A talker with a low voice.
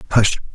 Yes: low, 105 Hz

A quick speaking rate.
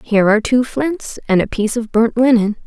Yes: fast, 225 wpm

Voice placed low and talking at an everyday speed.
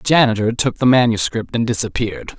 Yes: low, 115 Hz; average, 175 wpm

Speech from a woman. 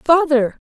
Yes: female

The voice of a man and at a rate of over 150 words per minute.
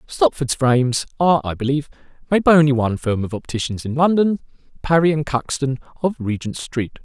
Yes: male; average, 170 wpm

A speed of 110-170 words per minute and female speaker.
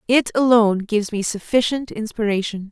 Yes: slow, 135 wpm; female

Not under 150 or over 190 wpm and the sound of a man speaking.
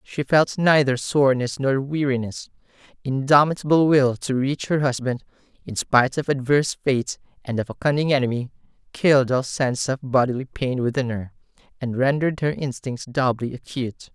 Yes: average, 155 wpm; male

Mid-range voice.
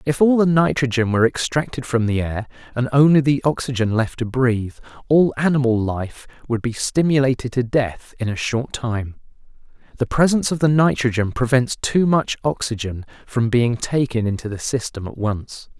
No: low, 125 Hz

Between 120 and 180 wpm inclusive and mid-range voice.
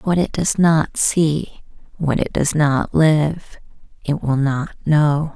Yes: average, 155 wpm; medium, 150 Hz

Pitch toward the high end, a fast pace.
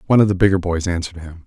No: very low, 90 Hz; fast, 285 wpm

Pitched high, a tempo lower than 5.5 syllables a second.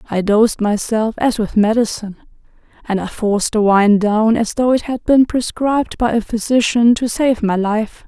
Yes: high, 225 Hz; 4.9 syllables/s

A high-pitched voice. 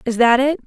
Yes: very high, 255 Hz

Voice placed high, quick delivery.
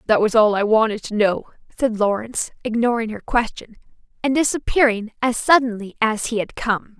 No: high, 225 Hz; average, 170 wpm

